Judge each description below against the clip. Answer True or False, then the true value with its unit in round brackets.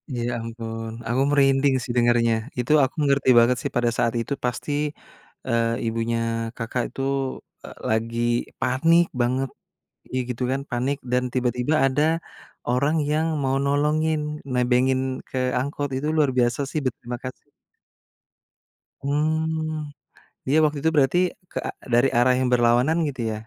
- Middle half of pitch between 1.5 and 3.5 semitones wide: True (3.2 semitones)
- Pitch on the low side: True (130 Hz)